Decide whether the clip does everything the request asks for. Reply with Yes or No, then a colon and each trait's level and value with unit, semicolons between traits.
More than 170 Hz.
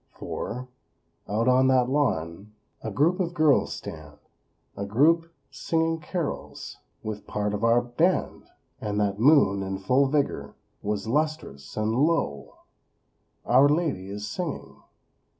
No: low, 125 Hz